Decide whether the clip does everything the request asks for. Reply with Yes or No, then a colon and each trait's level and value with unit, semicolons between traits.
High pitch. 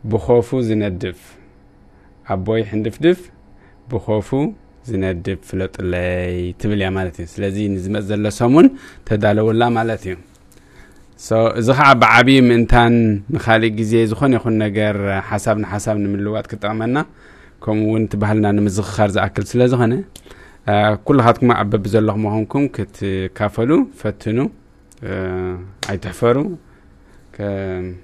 No: low, 105 Hz